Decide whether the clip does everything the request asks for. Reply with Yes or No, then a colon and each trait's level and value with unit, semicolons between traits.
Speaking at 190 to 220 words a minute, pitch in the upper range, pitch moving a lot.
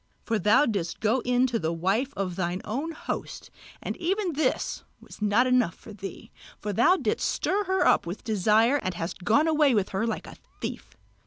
Yes: average, 195 wpm; high, 225 Hz; wide, 6.4 semitones